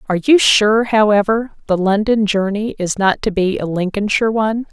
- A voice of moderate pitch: No, high, 210 Hz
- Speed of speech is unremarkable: Yes, average, 180 wpm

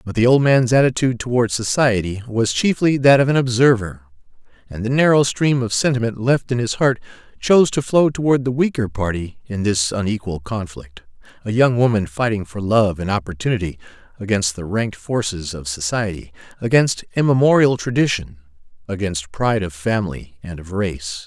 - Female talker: No, male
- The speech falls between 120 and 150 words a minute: No, average, 160 wpm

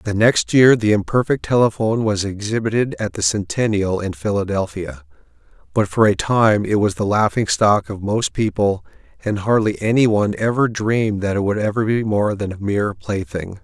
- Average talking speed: Yes, average, 175 wpm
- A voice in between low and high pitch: No, low, 105 Hz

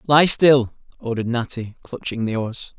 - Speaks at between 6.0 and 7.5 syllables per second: No, 4.6 syllables/s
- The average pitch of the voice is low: Yes, low, 125 Hz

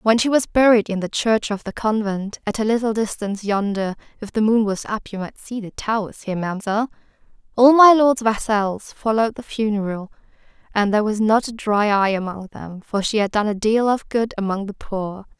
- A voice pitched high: Yes, high, 215 Hz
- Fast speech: Yes, fast, 210 wpm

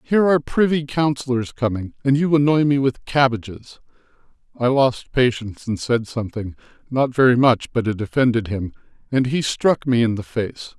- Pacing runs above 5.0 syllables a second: Yes, 5.2 syllables/s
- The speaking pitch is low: Yes, low, 125 Hz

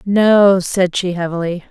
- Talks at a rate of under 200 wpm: Yes, average, 140 wpm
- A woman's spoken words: Yes, female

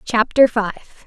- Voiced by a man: No, female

